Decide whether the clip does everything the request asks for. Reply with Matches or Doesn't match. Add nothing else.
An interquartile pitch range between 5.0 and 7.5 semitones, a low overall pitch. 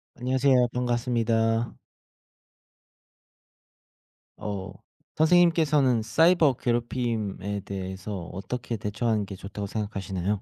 Doesn't match